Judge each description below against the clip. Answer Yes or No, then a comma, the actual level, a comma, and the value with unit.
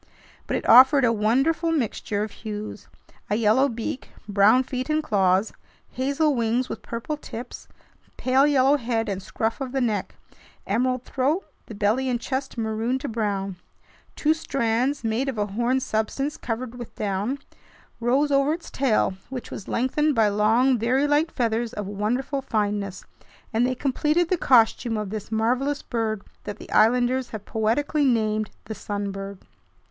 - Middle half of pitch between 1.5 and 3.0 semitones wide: No, average, 3.8 semitones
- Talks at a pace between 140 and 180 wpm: Yes, average, 160 wpm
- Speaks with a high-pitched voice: Yes, high, 235 Hz